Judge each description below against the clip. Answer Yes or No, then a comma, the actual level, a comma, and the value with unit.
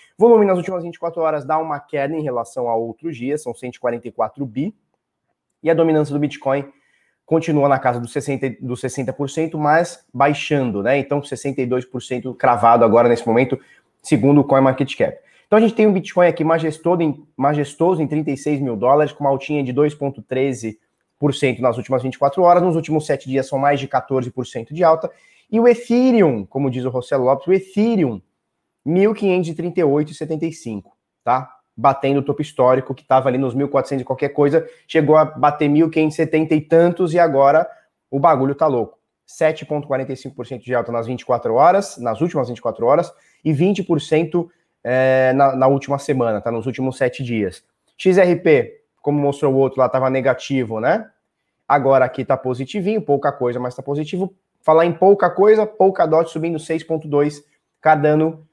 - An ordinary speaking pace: Yes, average, 165 wpm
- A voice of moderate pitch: Yes, medium, 145 Hz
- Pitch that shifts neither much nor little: Yes, average, 3.8 semitones